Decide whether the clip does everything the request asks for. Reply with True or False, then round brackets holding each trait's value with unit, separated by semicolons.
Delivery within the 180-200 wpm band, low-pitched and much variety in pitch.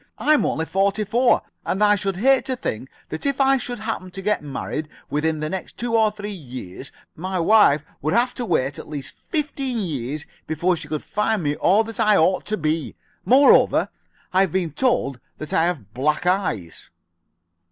False (190 wpm; 185 Hz; 6.4 semitones)